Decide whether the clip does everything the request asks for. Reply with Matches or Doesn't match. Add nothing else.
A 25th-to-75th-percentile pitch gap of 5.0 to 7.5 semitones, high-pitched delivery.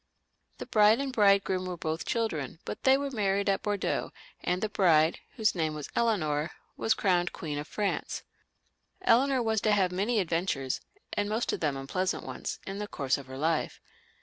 Matches